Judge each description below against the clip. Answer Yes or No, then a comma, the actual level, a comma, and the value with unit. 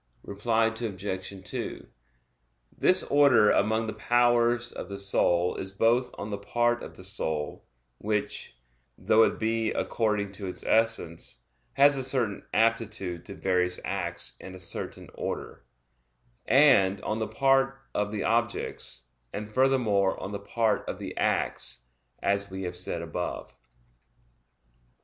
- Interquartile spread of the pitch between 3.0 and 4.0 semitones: Yes, average, 3.6 semitones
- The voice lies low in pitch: Yes, low, 105 Hz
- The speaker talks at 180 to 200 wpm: No, average, 140 wpm